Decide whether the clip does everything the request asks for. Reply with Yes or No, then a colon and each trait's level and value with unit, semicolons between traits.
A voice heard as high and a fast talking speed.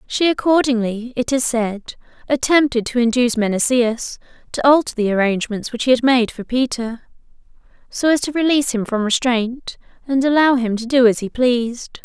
No: high, 245 Hz; average, 170 wpm